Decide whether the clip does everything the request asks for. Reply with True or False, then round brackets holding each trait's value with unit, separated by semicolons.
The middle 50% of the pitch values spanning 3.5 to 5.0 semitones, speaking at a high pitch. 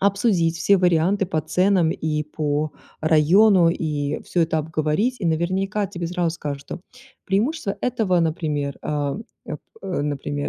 False (4.2 semitones; 165 Hz)